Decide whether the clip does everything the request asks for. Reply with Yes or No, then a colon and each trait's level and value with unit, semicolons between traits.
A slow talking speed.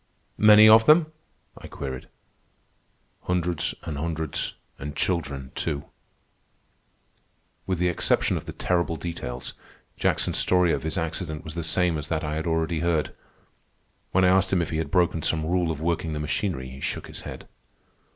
No: average, 165 wpm